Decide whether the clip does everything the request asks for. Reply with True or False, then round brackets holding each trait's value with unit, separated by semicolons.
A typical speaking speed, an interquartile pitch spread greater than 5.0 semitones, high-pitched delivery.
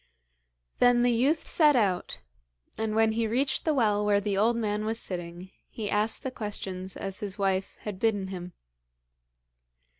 False (160 wpm; 3.2 semitones; 210 Hz)